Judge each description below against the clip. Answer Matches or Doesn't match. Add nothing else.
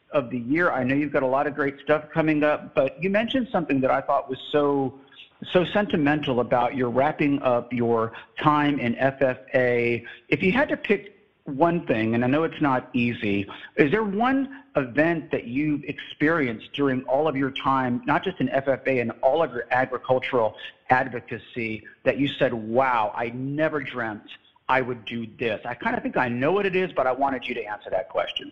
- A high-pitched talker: Doesn't match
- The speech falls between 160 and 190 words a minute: Doesn't match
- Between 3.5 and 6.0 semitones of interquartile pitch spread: Matches